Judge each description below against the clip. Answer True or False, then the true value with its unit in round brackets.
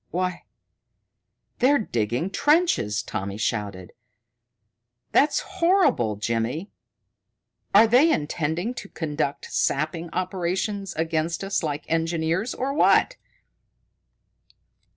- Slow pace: True (90 wpm)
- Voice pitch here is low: False (170 Hz)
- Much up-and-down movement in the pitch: True (6.6 semitones)